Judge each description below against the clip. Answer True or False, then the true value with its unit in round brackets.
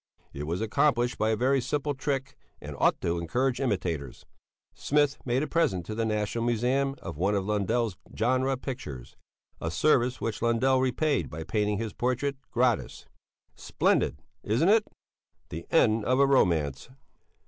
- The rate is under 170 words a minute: True (155 wpm)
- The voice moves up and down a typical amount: True (4.8 semitones)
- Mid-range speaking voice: False (120 Hz)